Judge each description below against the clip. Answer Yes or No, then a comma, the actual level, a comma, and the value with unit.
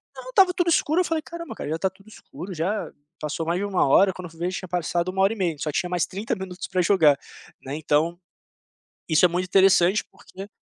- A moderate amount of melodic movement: Yes, average, 3.1 semitones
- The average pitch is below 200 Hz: Yes, medium, 185 Hz